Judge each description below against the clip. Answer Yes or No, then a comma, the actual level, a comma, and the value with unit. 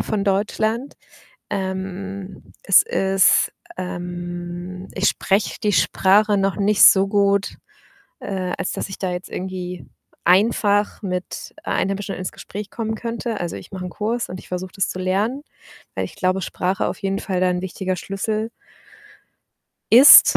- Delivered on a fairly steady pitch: Yes, narrow, 2.1 semitones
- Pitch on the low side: No, high, 195 Hz